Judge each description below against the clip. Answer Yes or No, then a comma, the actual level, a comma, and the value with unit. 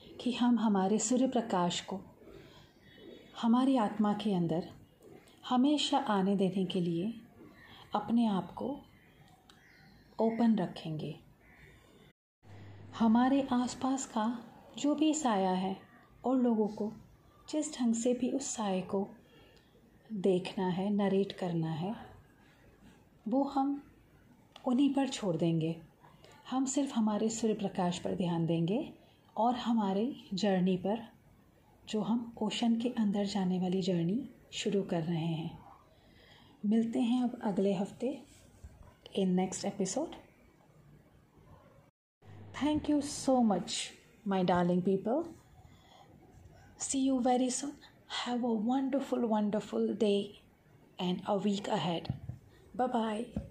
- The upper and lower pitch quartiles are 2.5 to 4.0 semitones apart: No, average, 4.9 semitones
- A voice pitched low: No, high, 215 Hz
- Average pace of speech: No, slow, 115 wpm